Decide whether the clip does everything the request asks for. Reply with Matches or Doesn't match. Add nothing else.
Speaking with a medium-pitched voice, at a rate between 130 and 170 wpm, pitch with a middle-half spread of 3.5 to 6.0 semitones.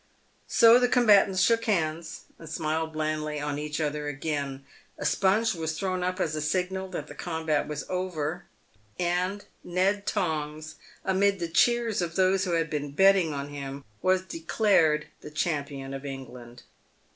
Matches